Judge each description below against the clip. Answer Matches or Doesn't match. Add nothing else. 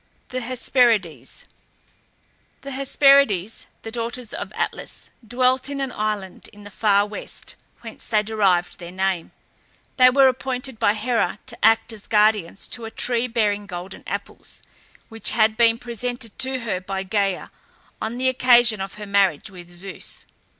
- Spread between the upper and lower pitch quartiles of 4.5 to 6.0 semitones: Doesn't match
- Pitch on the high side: Matches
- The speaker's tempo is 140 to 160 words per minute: Matches